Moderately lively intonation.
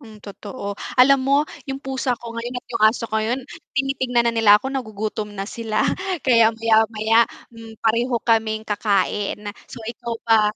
No: narrow, 2.2 semitones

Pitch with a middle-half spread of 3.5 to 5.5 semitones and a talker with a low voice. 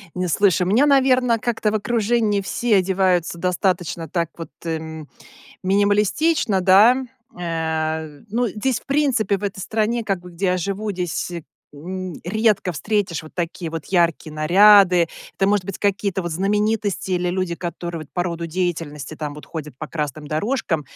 No: average, 3.9 semitones; medium, 185 Hz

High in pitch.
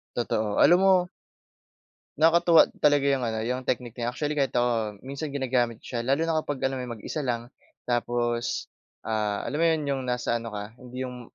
No: low, 125 Hz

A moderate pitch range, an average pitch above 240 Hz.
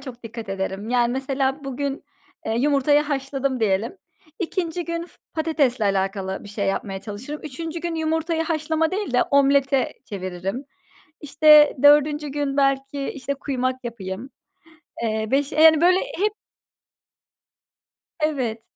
Yes: average, 4.8 semitones; very high, 275 Hz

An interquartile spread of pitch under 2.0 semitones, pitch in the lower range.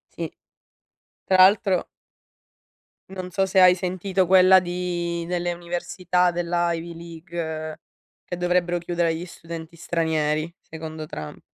No: narrow, 1.5 semitones; medium, 175 Hz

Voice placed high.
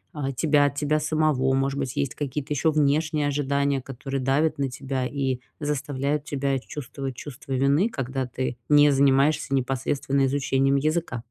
No: medium, 140 Hz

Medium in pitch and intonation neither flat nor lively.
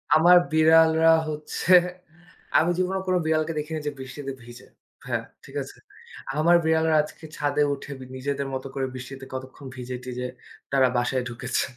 Yes: medium, 145 Hz; average, 3.5 semitones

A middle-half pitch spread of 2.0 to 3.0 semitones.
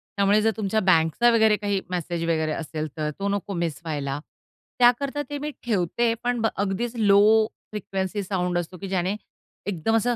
No: average, 4.6 semitones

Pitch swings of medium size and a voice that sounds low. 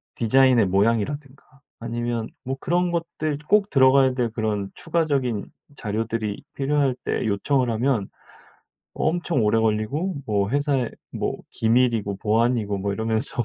Yes: average, 4.2 semitones; low, 120 Hz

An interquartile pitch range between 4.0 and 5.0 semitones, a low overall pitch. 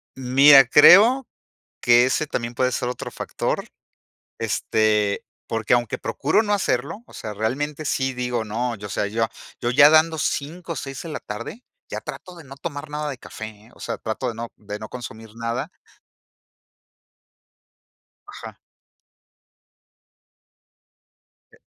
Yes: average, 4.7 semitones; low, 125 Hz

